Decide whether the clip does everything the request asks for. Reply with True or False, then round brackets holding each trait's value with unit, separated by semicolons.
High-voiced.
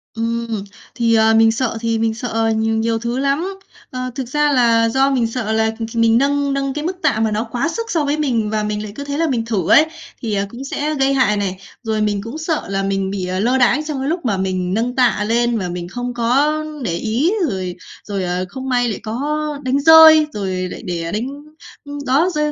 True (230 Hz)